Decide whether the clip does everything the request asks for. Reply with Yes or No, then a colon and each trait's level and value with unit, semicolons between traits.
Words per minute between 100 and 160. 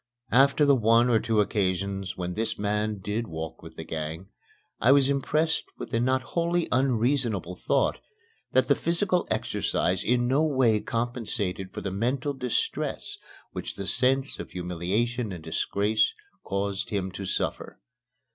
Yes: average, 150 wpm